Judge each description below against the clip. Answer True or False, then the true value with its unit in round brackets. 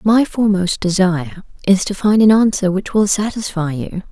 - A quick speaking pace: False (175 wpm)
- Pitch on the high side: True (195 Hz)